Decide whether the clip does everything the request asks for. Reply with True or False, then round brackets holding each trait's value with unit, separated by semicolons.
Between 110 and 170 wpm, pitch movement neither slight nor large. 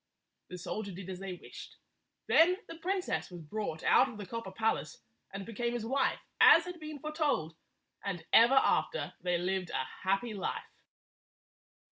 False (160 wpm; 7.0 semitones)